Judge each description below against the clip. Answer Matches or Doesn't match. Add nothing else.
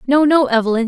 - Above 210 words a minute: Doesn't match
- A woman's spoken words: Matches